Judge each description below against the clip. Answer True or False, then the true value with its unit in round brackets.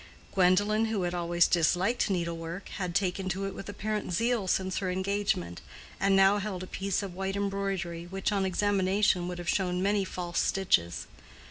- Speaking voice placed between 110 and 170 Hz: False (190 Hz)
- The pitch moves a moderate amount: False (2.1 semitones)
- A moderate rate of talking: True (170 wpm)